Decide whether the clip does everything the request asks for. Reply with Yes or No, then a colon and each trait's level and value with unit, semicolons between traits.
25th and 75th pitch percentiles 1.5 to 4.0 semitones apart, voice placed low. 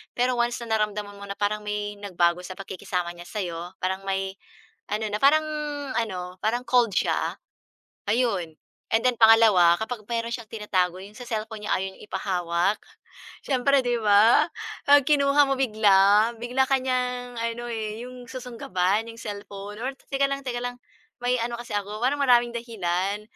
No: average, 3.7 semitones; high, 220 Hz